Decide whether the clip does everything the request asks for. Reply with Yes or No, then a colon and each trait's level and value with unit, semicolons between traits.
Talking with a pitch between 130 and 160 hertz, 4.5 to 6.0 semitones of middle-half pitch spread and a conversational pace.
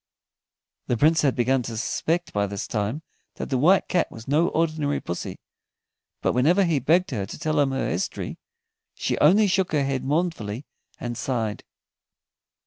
Yes: medium, 140 Hz; wide, 5.6 semitones; average, 165 wpm